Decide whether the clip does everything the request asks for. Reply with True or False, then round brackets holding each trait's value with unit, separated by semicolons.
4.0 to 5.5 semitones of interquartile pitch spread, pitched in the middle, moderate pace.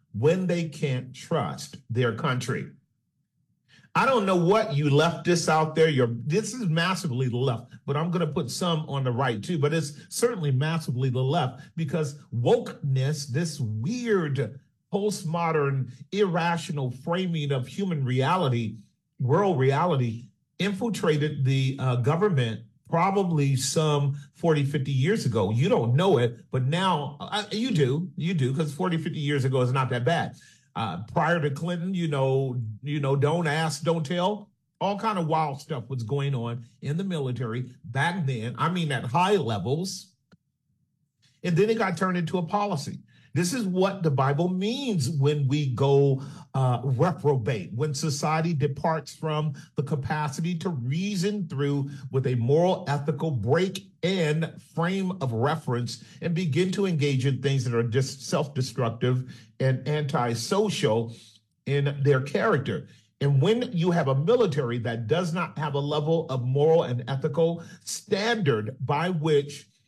True (4.5 semitones; 150 Hz; 155 wpm)